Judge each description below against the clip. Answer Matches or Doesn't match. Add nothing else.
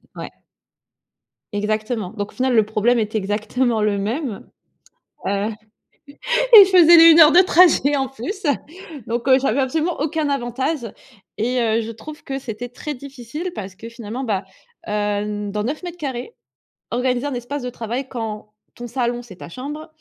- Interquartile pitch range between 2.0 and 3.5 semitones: Doesn't match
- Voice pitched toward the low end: Doesn't match